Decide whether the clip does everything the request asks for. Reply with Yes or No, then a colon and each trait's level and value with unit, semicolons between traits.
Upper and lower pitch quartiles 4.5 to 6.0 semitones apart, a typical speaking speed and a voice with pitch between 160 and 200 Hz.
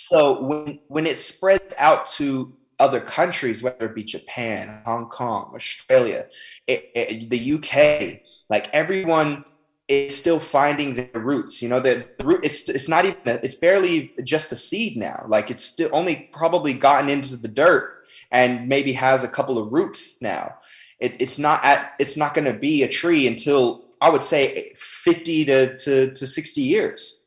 No: average, 5.1 semitones; average, 180 wpm; medium, 145 Hz